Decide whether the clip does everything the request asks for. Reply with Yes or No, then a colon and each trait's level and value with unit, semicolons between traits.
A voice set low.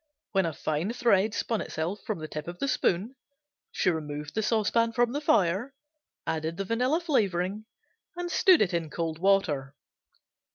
No: high, 195 Hz